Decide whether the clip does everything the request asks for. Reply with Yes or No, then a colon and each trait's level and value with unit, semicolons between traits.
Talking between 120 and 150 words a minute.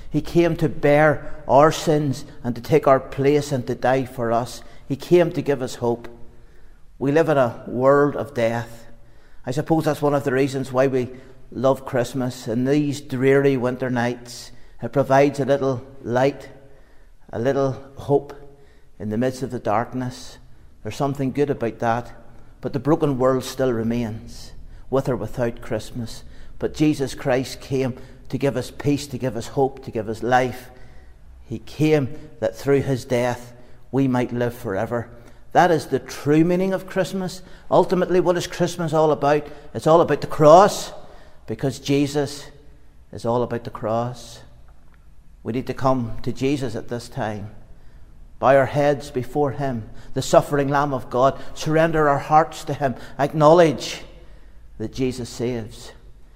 No: average, 165 wpm